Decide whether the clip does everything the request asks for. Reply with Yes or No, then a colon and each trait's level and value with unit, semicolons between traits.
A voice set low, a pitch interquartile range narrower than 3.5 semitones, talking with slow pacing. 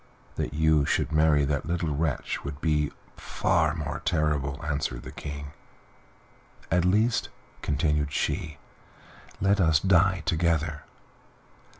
Yes: very low, 75 Hz; average, 2.7 semitones; slow, 115 wpm